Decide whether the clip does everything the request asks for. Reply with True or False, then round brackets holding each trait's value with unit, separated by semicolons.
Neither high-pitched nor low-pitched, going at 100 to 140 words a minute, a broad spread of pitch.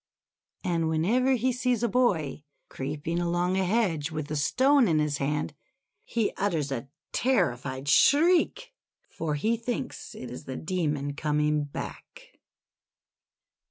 True (165 Hz; 135 wpm; 8.0 semitones)